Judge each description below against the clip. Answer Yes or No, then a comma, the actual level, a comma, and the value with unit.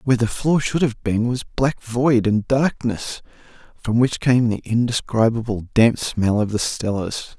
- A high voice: No, low, 115 Hz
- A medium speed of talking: Yes, average, 170 wpm